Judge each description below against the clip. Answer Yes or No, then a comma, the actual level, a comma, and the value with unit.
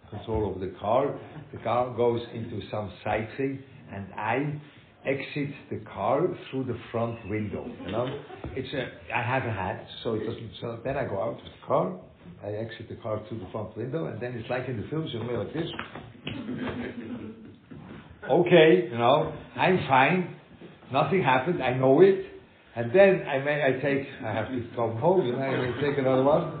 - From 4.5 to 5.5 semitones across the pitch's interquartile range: No, average, 3.7 semitones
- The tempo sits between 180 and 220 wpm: Yes, average, 200 wpm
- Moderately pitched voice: No, low, 125 Hz